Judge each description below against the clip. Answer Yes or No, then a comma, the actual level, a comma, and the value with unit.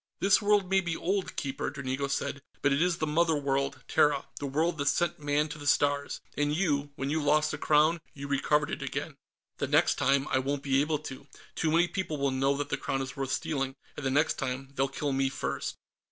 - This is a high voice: No, medium, 145 Hz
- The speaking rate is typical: No, fast, 225 wpm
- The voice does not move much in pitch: Yes, narrow, 2.3 semitones